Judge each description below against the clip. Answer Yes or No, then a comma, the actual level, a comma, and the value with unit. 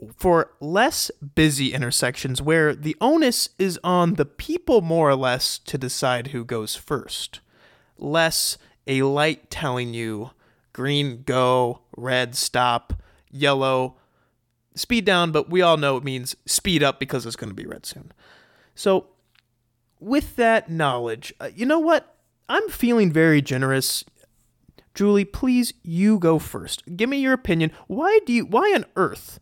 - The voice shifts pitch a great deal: Yes, wide, 7.2 semitones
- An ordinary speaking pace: Yes, average, 145 wpm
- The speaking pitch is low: No, medium, 145 Hz